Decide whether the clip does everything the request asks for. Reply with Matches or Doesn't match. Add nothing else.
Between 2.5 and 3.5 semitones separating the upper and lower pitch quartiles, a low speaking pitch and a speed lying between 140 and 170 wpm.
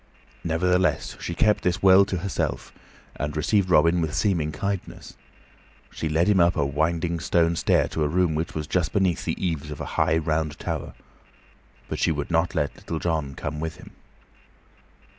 Doesn't match